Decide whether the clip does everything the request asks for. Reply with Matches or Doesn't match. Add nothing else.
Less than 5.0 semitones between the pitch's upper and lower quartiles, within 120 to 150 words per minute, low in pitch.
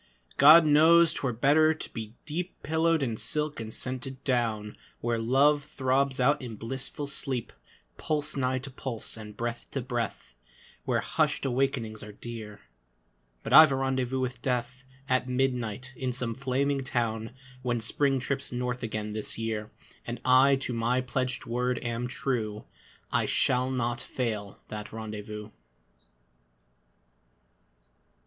Matches